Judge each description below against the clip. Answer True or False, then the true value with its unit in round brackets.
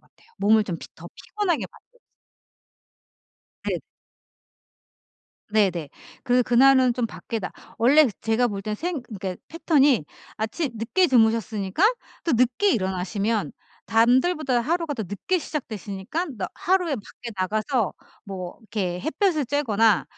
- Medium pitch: False (230 Hz)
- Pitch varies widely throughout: True (6.1 semitones)